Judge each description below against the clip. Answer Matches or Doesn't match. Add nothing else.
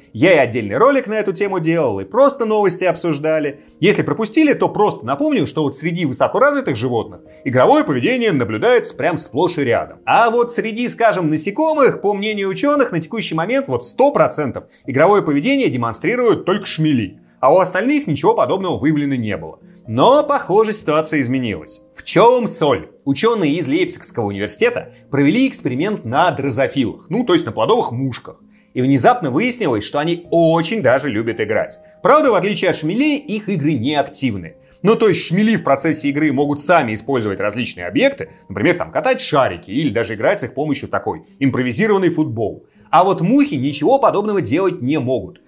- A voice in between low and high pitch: Matches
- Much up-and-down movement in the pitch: Matches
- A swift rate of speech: Matches